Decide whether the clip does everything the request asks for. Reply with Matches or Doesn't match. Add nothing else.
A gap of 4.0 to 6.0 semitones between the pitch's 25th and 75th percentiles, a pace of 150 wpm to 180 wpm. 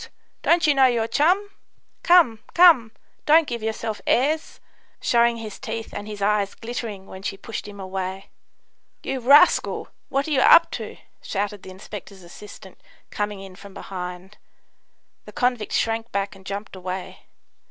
Matches